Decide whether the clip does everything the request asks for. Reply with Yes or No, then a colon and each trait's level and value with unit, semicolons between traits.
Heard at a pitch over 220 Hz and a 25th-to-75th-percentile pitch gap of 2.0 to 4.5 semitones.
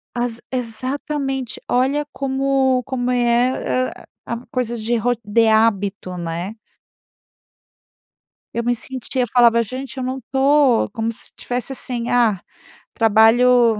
Yes: high, 245 Hz; narrow, 2.4 semitones